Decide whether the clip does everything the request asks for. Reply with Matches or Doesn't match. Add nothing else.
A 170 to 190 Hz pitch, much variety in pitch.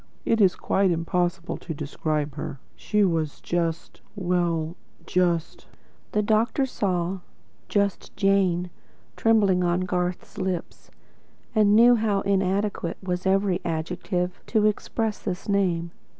Doesn't match